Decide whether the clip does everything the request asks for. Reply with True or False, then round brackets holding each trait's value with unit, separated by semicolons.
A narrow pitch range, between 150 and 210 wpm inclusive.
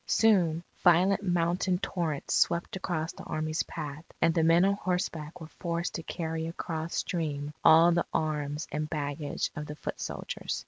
True (2.1 semitones; 165 wpm)